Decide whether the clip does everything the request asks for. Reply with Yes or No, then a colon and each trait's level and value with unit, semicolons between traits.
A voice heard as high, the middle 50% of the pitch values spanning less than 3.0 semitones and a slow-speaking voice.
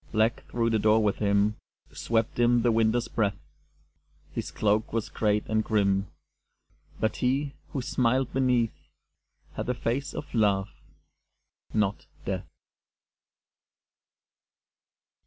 No: low, 110 Hz; narrow, 2.4 semitones; slow, 120 wpm